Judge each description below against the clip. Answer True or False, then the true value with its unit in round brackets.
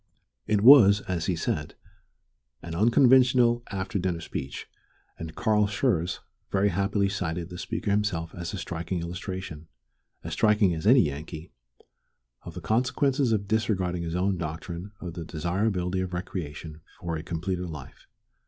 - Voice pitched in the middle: False (95 Hz)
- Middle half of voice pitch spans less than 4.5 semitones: True (4.0 semitones)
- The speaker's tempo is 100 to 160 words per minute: True (145 wpm)